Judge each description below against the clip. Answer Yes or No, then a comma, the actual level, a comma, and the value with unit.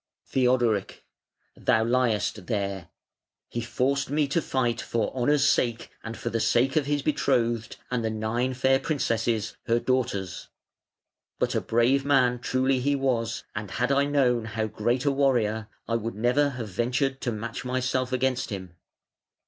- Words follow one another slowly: No, average, 155 wpm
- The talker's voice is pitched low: Yes, low, 120 Hz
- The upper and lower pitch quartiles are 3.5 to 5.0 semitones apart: No, average, 3.0 semitones